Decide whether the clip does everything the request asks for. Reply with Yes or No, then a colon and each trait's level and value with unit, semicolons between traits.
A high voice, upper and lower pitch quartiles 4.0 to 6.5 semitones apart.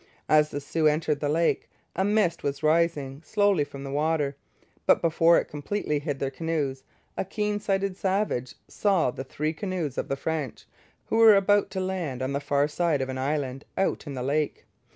No: medium, 155 Hz; average, 4.9 semitones